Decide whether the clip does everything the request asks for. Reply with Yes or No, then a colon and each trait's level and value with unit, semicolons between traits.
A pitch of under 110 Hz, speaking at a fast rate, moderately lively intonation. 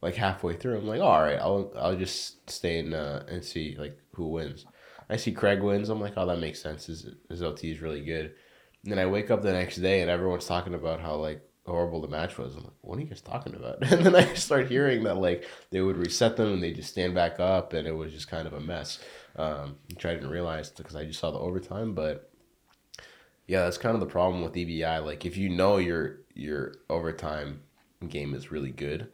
Yes: very low, 85 Hz; fast, 240 wpm; average, 3.2 semitones